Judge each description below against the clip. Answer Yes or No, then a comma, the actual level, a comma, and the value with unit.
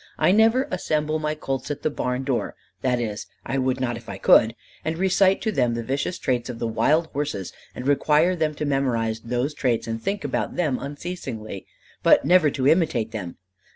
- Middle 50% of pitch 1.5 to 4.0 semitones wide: No, average, 5.0 semitones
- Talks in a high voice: No, low, 135 Hz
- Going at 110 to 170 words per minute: No, average, 195 wpm